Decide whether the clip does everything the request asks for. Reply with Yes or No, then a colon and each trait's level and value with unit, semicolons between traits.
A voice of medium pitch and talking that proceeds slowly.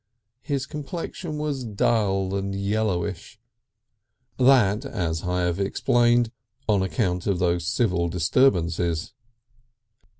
No: low, 100 Hz; slow, 100 wpm